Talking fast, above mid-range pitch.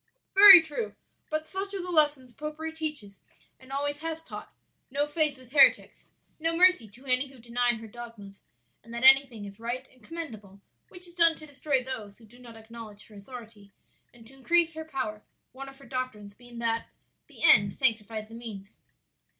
No: average, 185 wpm; very high, 255 Hz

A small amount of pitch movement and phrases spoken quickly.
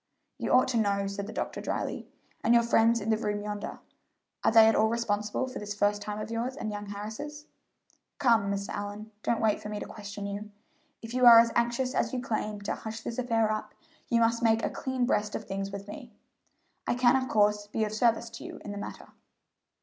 Yes: narrow, 2.2 semitones; fast, 225 wpm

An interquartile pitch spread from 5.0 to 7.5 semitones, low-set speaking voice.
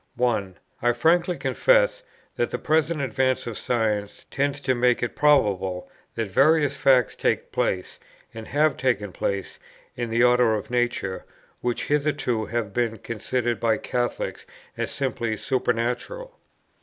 No: average, 4.0 semitones; low, 120 Hz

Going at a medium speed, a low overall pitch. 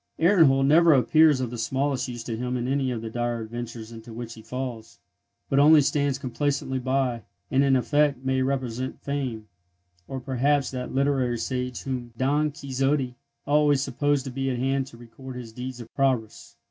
Yes: average, 180 wpm; low, 130 Hz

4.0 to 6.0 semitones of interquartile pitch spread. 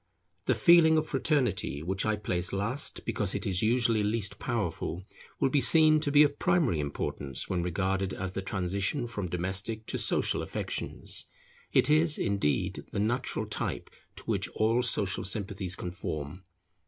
Yes: wide, 5.5 semitones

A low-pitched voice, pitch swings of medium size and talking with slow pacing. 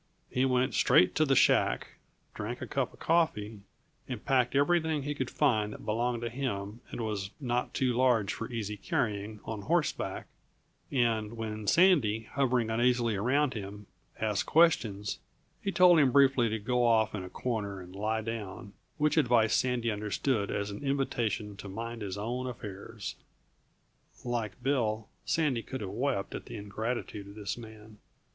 No: low, 115 Hz; average, 3.6 semitones; average, 165 wpm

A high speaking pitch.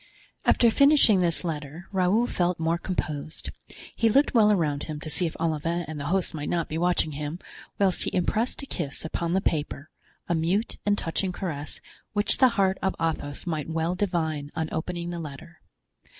No: medium, 170 Hz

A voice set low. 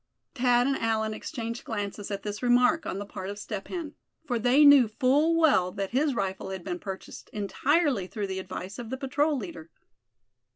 No: high, 225 Hz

